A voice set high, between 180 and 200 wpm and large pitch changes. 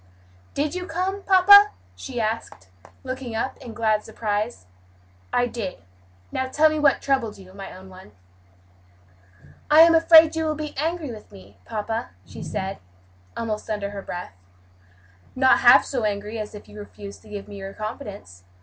No: high, 225 Hz; average, 165 wpm; wide, 6.6 semitones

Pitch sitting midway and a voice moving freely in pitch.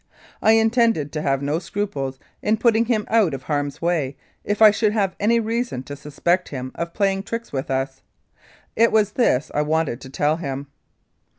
Yes: medium, 170 Hz; wide, 7.5 semitones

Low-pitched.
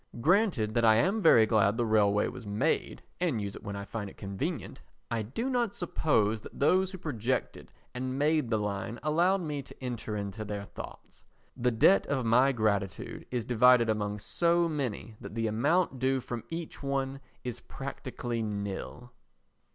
Yes: low, 120 Hz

